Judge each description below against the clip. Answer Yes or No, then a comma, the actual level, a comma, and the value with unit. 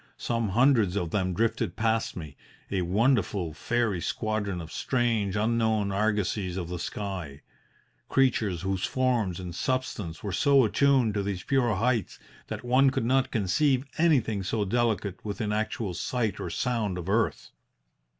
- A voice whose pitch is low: Yes, low, 105 Hz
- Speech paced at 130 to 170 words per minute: Yes, average, 150 wpm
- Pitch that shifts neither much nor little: Yes, average, 4.2 semitones